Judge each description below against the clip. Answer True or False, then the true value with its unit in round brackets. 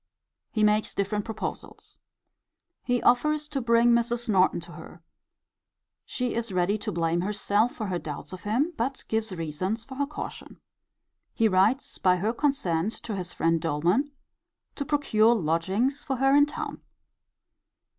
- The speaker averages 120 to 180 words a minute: True (150 wpm)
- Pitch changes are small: False (5.2 semitones)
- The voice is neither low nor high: False (220 Hz)